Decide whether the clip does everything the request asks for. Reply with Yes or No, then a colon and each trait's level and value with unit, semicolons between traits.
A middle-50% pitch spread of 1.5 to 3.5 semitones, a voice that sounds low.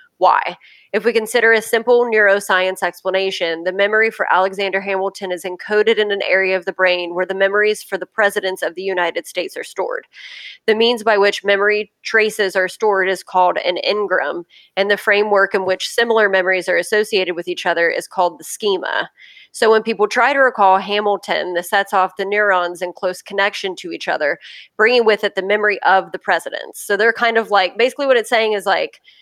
No: average, 2.9 semitones; high, 200 Hz